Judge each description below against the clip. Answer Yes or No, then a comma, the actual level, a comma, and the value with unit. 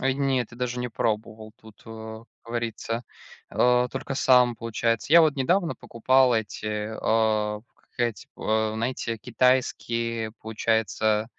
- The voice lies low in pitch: Yes, low, 115 Hz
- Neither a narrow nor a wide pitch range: No, narrow, 2.2 semitones